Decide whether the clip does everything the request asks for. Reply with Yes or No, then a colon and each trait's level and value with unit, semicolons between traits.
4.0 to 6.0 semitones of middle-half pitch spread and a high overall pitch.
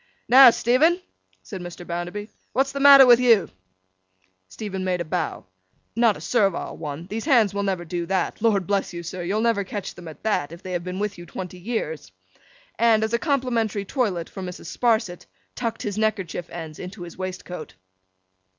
Yes: average, 4.5 semitones; high, 195 Hz